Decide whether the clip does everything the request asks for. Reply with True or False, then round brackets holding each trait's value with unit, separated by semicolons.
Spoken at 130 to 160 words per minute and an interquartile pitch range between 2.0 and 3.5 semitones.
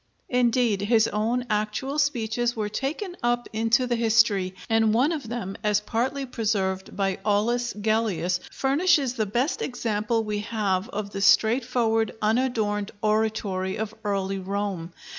True (140 wpm; 2.8 semitones)